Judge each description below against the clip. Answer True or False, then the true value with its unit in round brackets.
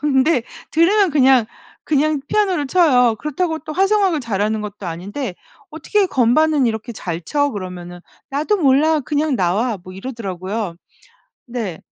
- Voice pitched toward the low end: False (260 Hz)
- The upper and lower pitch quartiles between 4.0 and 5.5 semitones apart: False (6.8 semitones)